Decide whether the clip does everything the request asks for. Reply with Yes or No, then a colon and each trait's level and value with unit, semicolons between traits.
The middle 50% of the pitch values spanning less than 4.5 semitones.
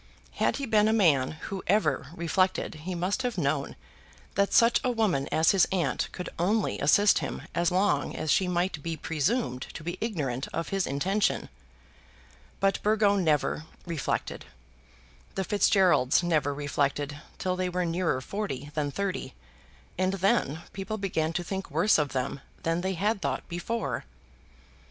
No: average, 4.8 semitones